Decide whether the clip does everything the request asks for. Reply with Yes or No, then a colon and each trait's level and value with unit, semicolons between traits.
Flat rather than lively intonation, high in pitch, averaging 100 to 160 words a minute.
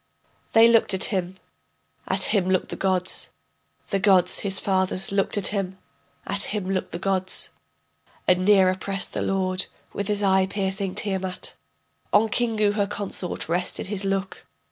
Yes: narrow, 1.4 semitones; high, 195 Hz; average, 155 wpm